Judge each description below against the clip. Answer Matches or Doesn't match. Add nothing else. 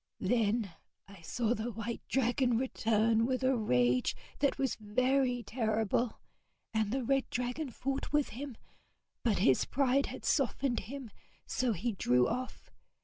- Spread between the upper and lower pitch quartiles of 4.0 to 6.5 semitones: Doesn't match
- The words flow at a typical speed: Matches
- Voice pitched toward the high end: Matches